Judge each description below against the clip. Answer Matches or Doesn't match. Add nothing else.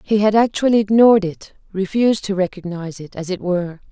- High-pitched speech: Matches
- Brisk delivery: Doesn't match